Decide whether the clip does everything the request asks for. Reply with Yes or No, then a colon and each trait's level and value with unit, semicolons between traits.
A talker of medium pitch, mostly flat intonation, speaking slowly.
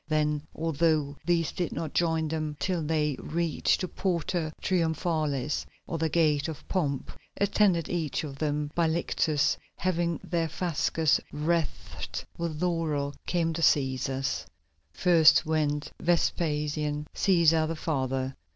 Yes: medium, 160 Hz; narrow, 2.2 semitones; slow, 125 wpm